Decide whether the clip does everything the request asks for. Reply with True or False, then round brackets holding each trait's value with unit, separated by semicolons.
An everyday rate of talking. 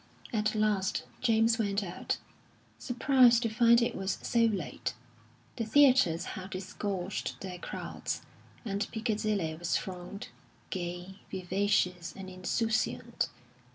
False (115 wpm)